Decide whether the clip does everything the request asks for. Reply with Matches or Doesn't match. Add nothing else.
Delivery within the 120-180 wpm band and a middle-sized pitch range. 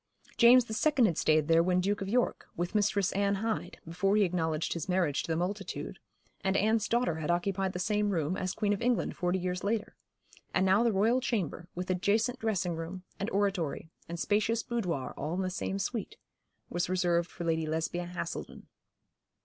Doesn't match